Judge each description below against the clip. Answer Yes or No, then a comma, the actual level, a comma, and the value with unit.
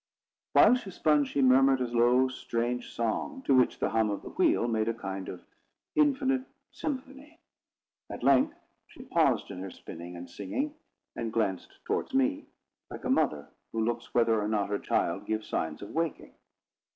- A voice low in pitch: Yes, low, 125 Hz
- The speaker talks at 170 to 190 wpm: Yes, average, 175 wpm